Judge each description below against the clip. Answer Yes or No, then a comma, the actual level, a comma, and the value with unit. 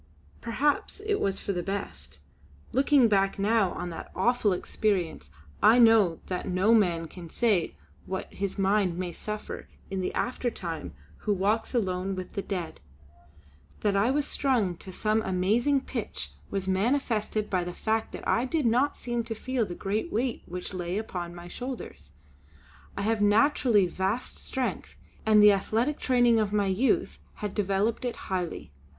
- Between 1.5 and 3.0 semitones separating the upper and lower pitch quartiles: No, average, 4.1 semitones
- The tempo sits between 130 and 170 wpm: Yes, average, 160 wpm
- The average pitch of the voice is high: Yes, high, 205 Hz